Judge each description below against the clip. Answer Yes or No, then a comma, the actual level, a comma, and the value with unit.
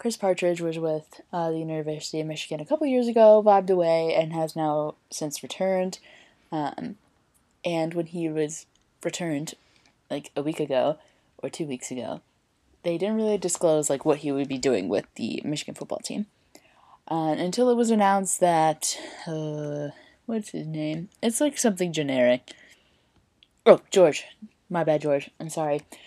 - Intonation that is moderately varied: Yes, average, 4.2 semitones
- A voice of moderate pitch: Yes, medium, 165 Hz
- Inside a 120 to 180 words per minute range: Yes, average, 160 wpm